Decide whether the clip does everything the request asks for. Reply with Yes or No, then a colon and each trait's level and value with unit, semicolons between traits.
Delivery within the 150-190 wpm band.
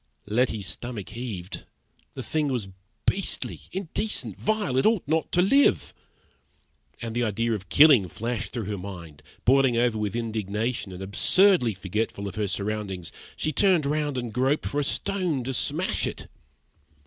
Yes: average, 155 wpm